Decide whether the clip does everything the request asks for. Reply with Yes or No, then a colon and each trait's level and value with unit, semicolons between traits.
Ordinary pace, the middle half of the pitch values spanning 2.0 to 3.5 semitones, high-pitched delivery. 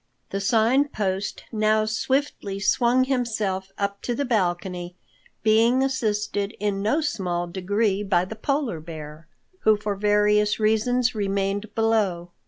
No: slow, 130 wpm; average, 2.7 semitones; high, 210 Hz